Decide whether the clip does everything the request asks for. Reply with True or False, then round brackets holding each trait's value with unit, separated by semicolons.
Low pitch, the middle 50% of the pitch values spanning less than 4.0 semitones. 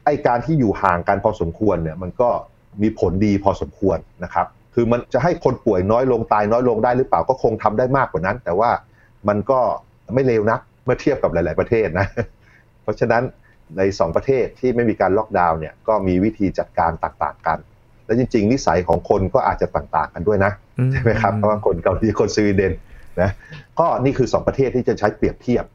True (105 Hz; 3.5 semitones)